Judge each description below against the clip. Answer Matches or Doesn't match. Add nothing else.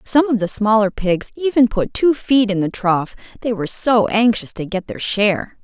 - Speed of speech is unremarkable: Doesn't match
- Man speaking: Doesn't match